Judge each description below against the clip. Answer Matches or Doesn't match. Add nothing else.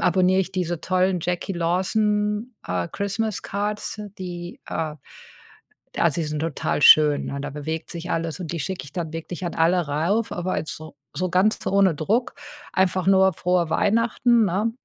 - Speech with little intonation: Doesn't match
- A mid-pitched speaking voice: Matches